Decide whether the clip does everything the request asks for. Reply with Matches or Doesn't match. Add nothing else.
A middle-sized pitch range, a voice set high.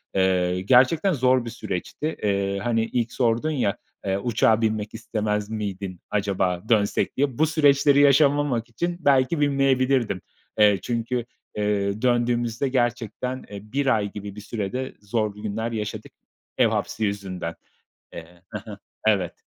Doesn't match